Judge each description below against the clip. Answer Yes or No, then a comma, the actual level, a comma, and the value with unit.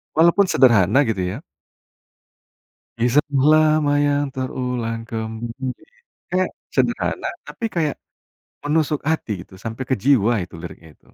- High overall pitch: No, low, 130 Hz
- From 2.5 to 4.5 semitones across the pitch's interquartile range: No, average, 5.0 semitones